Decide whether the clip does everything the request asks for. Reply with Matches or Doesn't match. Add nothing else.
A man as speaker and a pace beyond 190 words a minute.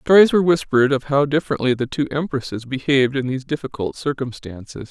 Doesn't match